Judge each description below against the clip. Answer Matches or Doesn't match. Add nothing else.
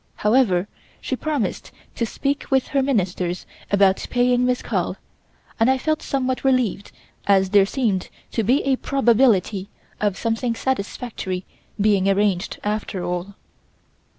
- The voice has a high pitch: Matches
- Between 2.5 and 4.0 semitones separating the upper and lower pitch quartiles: Doesn't match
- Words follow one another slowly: Matches